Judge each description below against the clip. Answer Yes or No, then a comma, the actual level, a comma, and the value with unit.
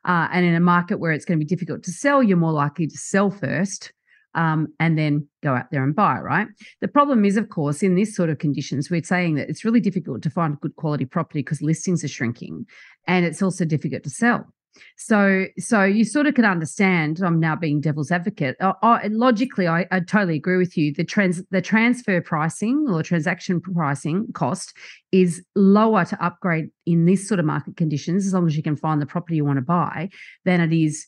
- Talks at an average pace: No, fast, 220 wpm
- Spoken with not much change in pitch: No, average, 3.8 semitones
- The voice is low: No, medium, 175 Hz